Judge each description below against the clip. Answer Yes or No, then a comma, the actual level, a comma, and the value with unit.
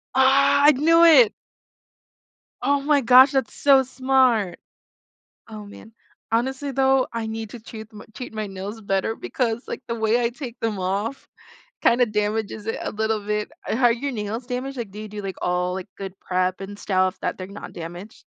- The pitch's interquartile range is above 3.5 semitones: Yes, average, 4.1 semitones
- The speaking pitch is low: No, high, 225 Hz